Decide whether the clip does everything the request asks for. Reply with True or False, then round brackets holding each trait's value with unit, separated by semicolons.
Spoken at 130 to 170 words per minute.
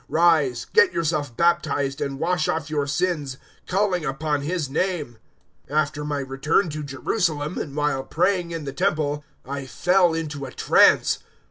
True (155 wpm)